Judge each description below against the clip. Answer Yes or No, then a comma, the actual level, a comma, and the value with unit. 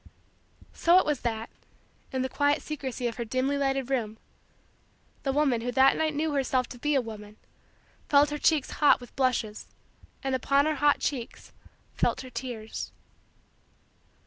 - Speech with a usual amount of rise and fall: Yes, average, 3.1 semitones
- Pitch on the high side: Yes, very high, 265 Hz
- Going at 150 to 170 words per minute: Yes, average, 160 wpm